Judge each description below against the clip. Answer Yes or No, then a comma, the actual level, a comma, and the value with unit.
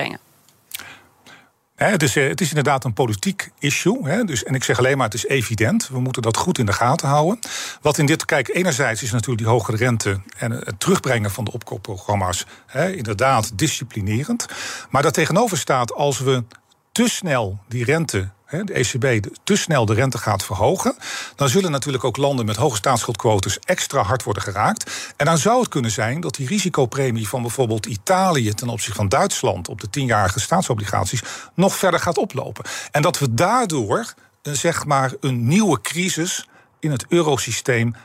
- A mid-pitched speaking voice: No, low, 130 Hz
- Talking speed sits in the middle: Yes, average, 175 wpm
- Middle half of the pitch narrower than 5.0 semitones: No, wide, 5.4 semitones